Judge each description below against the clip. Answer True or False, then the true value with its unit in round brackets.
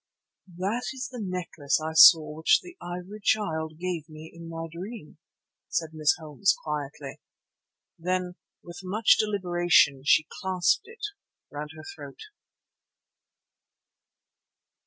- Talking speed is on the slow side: True (115 wpm)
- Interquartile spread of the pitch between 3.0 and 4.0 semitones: True (3.3 semitones)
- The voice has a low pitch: False (170 Hz)